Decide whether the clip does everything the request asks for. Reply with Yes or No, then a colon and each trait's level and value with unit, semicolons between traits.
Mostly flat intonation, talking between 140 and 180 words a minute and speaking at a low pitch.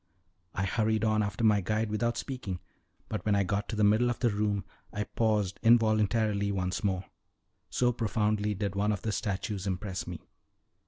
Yes: narrow, 1.7 semitones; average, 175 wpm; low, 105 Hz